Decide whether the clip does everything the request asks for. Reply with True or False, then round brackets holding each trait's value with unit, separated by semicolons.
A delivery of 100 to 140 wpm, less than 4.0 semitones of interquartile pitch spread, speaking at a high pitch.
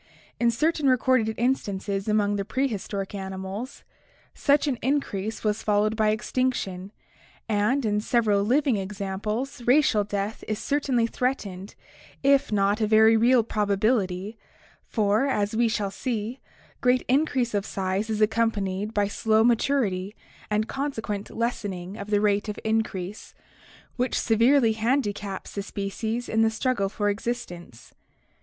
True (135 wpm; 3.1 semitones; 215 Hz)